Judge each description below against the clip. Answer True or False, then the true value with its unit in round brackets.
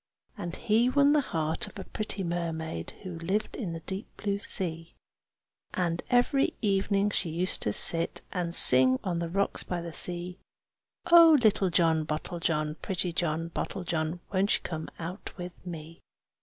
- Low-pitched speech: False (175 Hz)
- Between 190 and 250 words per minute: False (160 wpm)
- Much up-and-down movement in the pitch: False (3.3 semitones)